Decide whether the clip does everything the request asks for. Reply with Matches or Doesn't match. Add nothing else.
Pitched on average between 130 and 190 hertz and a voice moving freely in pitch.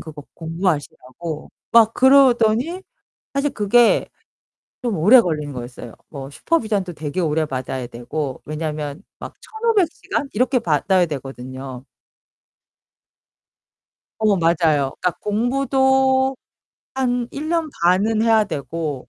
Matches